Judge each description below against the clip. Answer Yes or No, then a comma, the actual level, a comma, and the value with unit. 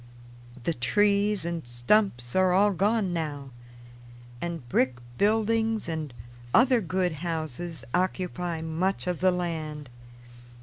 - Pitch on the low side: No, medium, 175 Hz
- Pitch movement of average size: Yes, average, 4.2 semitones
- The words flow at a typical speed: No, slow, 115 wpm